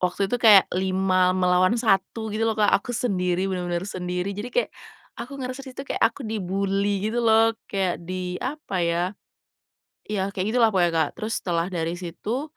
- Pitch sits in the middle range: No, high, 195 Hz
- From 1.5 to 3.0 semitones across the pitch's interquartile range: No, average, 3.7 semitones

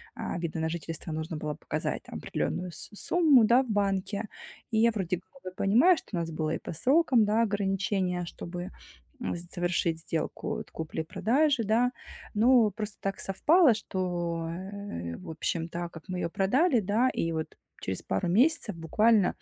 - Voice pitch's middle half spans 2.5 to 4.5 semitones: No, average, 5.1 semitones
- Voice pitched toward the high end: Yes, high, 195 Hz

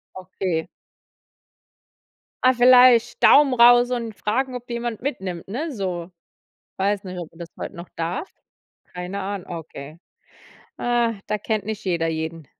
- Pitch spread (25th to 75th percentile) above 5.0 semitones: Yes, wide, 5.6 semitones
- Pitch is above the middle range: Yes, high, 200 Hz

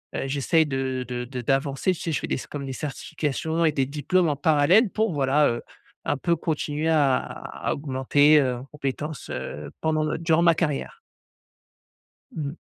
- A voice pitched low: No, medium, 145 Hz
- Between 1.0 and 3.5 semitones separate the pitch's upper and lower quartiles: Yes, average, 2.9 semitones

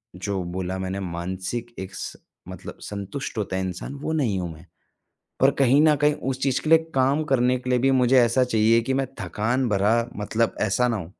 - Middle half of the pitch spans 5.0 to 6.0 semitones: Yes, wide, 5.6 semitones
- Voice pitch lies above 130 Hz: No, low, 115 Hz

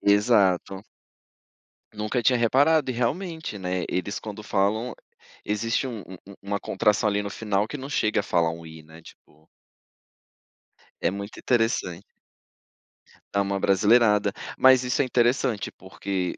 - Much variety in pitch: No, average, 3.7 semitones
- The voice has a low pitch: Yes, low, 105 Hz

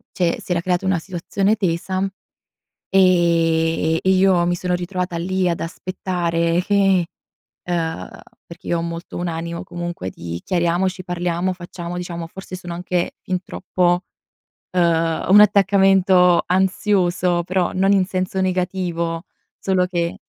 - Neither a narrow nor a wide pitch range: No, narrow, 1.6 semitones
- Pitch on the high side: No, medium, 180 Hz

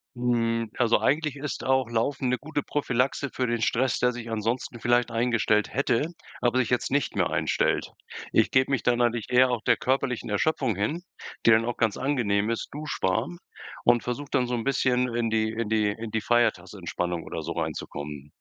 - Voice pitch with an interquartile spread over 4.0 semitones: No, average, 2.8 semitones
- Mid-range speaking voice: No, low, 120 Hz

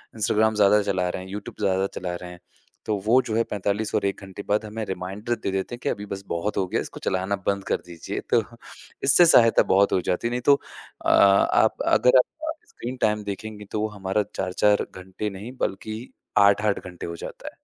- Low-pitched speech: Yes, low, 100 Hz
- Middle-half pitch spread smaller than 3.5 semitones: Yes, narrow, 2.5 semitones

